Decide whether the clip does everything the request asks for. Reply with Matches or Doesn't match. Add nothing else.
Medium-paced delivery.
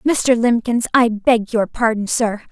Matches